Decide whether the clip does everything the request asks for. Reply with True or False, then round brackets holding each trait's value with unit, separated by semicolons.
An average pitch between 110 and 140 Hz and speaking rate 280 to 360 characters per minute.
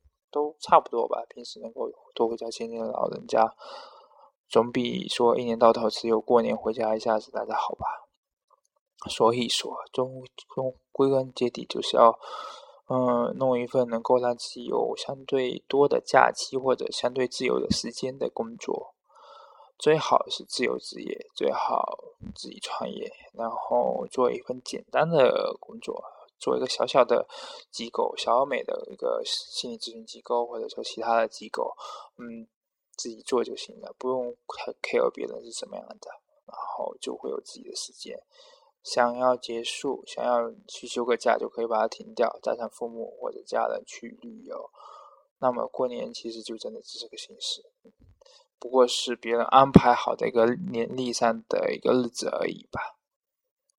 False (135 Hz; 245 characters per minute)